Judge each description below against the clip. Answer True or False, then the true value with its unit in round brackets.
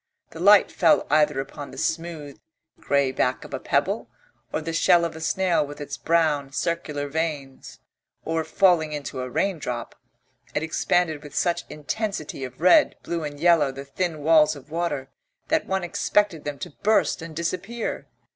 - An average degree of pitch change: True (3.1 semitones)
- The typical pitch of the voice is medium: True (160 Hz)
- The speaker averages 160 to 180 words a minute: True (165 wpm)